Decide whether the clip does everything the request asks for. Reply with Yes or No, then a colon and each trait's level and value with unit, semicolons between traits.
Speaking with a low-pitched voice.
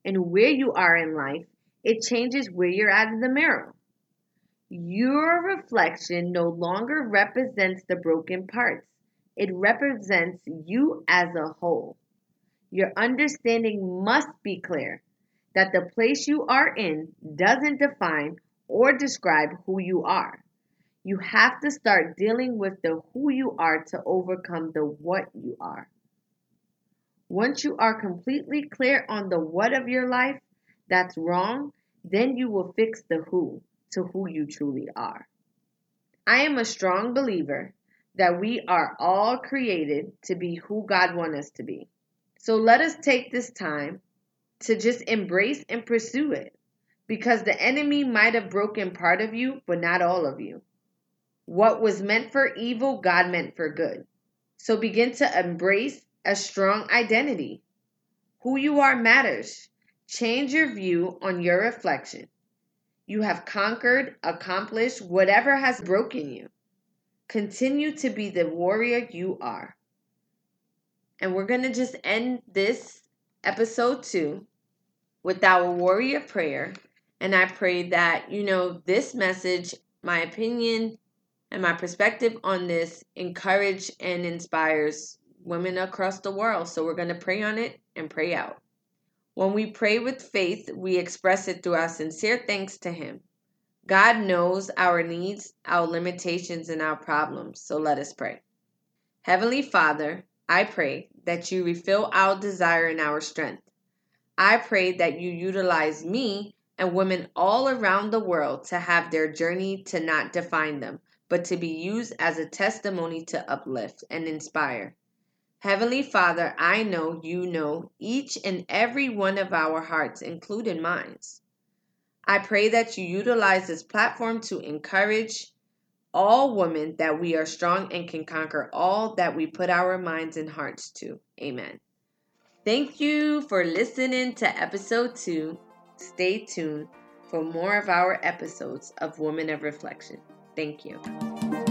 No: high, 195 Hz